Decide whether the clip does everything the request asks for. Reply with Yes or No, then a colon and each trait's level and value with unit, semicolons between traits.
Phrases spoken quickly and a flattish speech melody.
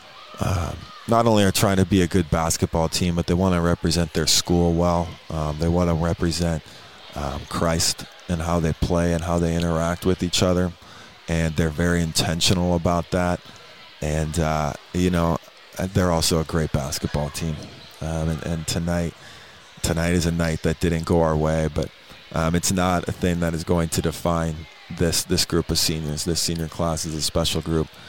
No: average, 190 wpm; narrow, 1.5 semitones